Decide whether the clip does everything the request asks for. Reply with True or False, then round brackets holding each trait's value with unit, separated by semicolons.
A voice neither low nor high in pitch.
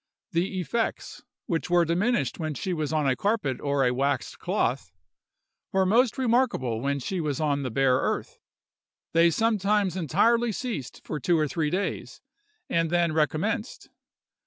True (170 Hz)